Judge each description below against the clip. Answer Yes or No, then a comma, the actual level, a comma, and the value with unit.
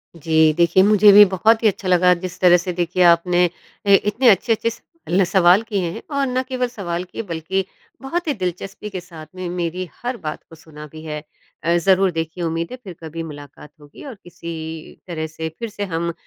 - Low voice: No, medium, 180 Hz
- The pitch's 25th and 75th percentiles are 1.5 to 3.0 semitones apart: No, average, 3.5 semitones